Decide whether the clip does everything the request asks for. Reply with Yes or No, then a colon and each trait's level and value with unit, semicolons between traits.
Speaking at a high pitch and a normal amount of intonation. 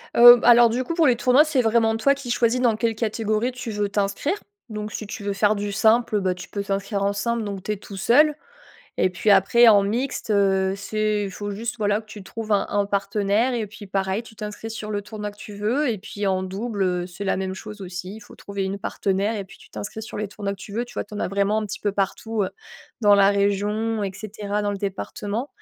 No: high, 210 Hz; narrow, 2.2 semitones